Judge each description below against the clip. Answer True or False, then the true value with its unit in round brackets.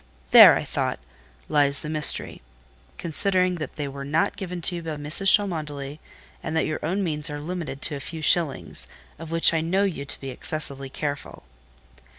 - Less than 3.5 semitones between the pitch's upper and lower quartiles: True (3.0 semitones)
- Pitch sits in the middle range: True (155 Hz)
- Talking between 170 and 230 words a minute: True (175 wpm)